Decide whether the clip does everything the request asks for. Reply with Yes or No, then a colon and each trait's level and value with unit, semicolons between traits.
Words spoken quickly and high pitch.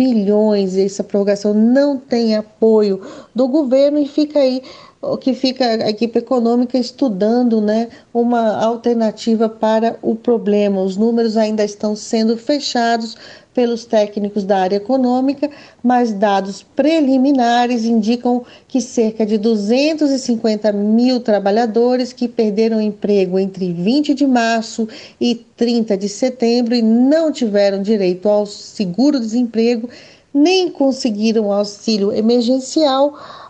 No: slow, 120 wpm; high, 230 Hz